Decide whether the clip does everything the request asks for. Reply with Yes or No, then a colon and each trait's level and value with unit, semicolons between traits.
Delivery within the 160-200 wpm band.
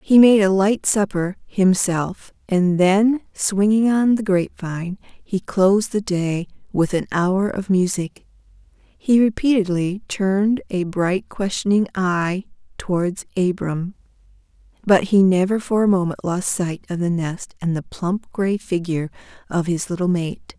No: average, 150 wpm